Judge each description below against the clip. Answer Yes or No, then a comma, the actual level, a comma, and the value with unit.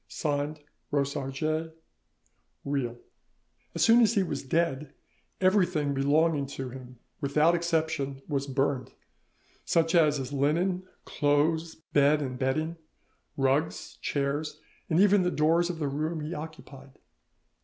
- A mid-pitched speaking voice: Yes, medium, 150 Hz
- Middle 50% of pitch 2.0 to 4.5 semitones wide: Yes, average, 2.9 semitones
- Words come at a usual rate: No, slow, 120 wpm